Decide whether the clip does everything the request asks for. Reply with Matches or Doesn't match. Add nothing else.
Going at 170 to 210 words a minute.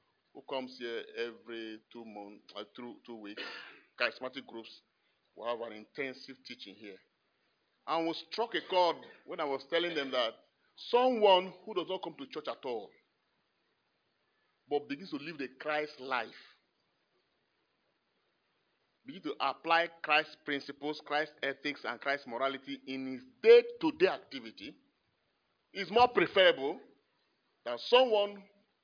Doesn't match